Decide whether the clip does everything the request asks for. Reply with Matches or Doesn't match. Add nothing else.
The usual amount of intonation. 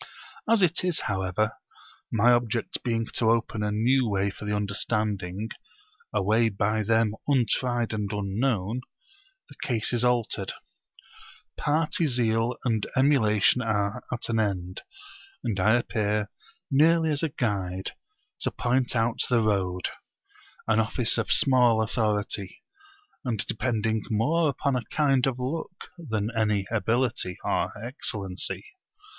Matches